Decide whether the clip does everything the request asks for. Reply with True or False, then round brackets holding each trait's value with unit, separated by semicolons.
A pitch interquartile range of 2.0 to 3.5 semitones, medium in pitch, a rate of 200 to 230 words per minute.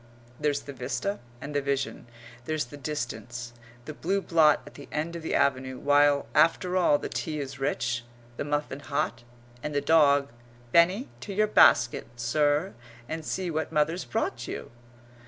False (2.8 semitones; 145 Hz; 165 wpm)